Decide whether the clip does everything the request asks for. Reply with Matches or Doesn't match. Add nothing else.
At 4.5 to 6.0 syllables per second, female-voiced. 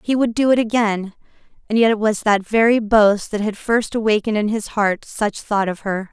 Matches